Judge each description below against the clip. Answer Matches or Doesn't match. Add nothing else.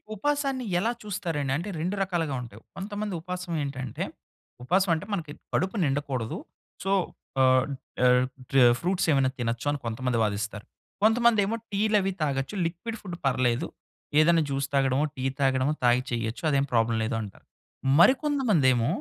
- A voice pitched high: Doesn't match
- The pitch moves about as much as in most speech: Doesn't match